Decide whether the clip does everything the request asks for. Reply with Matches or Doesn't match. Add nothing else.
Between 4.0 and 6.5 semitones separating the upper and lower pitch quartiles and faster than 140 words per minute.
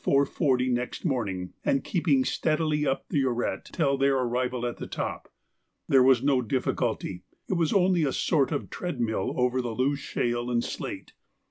Doesn't match